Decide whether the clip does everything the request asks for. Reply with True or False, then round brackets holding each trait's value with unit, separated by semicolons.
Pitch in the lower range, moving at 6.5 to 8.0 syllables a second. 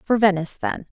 False (200 Hz; 6.6 syllables/s)